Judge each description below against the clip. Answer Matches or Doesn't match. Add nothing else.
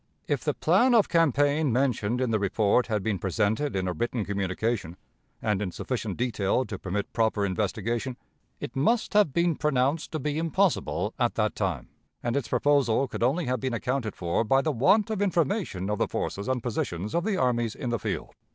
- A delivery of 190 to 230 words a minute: Matches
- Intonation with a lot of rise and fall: Matches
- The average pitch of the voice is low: Matches